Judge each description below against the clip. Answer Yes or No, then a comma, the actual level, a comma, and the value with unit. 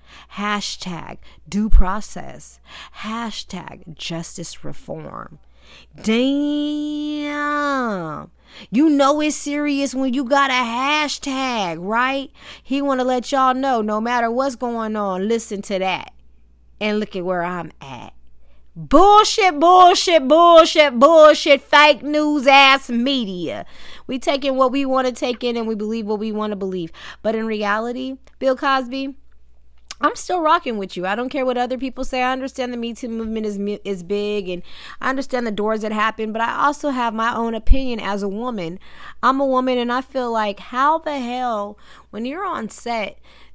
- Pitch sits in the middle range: No, high, 245 Hz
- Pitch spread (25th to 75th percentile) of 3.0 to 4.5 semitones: No, average, 4.9 semitones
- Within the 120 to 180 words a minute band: Yes, average, 165 wpm